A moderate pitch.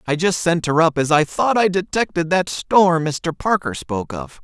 Yes: medium, 165 Hz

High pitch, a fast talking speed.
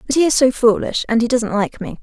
Yes: high, 245 Hz; fast, 295 wpm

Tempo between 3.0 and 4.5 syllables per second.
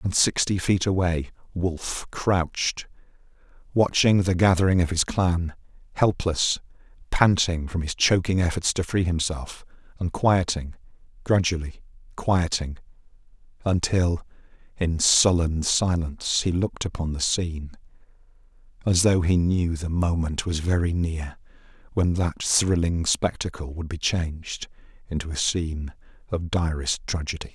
Yes: 4.4 syllables/s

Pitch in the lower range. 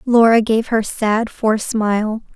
No: high, 220 Hz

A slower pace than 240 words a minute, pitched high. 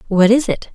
No: fast, 245 wpm; high, 210 Hz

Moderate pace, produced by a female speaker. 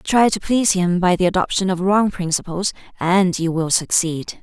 Yes: average, 190 wpm; female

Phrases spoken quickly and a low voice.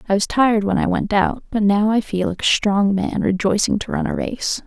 No: fast, 255 wpm; high, 205 Hz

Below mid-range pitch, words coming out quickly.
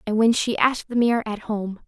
No: high, 220 Hz; fast, 255 wpm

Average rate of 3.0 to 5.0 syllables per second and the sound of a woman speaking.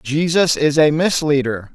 No: 4.1 syllables/s; male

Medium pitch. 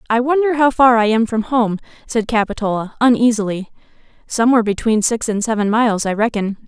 No: high, 225 Hz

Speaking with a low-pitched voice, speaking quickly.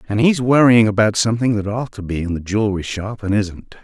Yes: low, 105 Hz; fast, 235 wpm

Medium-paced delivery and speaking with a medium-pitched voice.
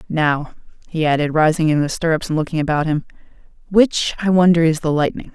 Yes: average, 190 wpm; medium, 160 Hz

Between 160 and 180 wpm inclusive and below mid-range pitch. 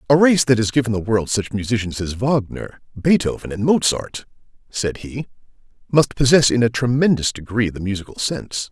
Yes: average, 170 wpm; low, 115 Hz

